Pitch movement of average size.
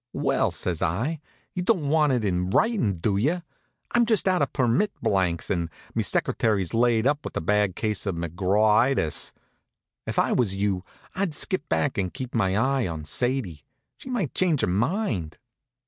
No: wide, 7.9 semitones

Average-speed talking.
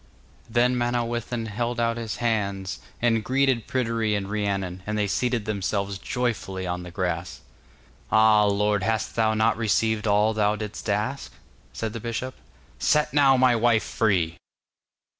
Yes: average, 145 wpm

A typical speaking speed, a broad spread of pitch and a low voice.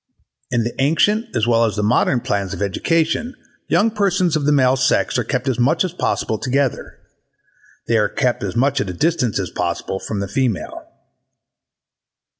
Yes: average, 180 wpm; wide, 6.9 semitones; low, 125 Hz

